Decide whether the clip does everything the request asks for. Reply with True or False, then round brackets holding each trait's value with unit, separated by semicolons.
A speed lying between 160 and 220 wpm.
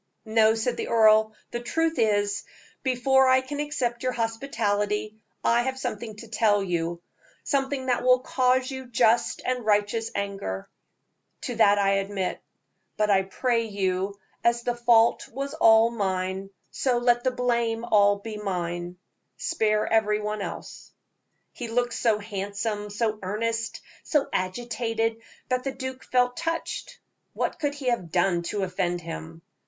False (150 wpm)